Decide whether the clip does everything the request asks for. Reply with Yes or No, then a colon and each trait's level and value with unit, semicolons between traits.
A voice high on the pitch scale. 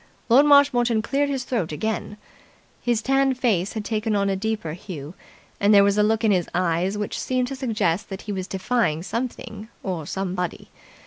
Yes: high, 210 Hz